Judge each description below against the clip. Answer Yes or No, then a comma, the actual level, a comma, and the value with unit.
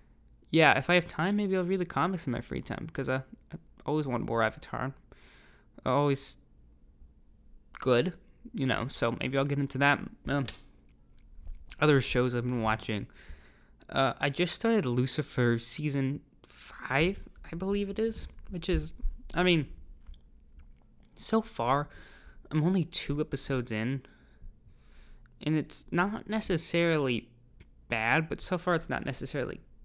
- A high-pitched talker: No, low, 135 Hz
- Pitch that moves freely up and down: Yes, wide, 6.8 semitones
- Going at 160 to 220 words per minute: No, average, 140 wpm